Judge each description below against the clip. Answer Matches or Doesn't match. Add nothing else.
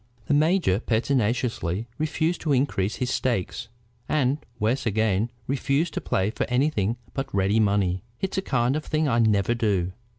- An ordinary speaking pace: Matches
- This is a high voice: Doesn't match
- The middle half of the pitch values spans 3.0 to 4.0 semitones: Doesn't match